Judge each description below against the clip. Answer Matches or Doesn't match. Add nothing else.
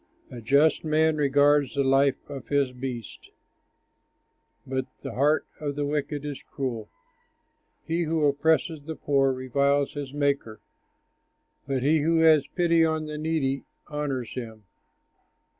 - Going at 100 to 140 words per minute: Matches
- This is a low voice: Doesn't match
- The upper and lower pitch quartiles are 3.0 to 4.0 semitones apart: Doesn't match